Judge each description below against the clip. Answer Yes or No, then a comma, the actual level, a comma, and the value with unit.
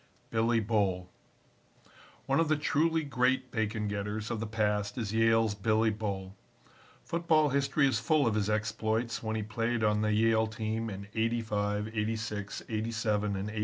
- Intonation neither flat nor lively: No, narrow, 1.9 semitones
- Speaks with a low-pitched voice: Yes, low, 110 Hz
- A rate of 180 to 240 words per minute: No, average, 160 wpm